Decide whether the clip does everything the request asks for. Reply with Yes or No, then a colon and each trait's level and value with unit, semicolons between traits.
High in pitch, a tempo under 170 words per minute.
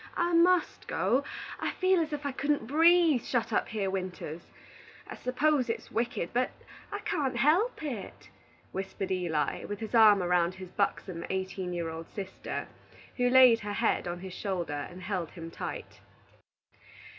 Yes: high, 210 Hz; average, 160 wpm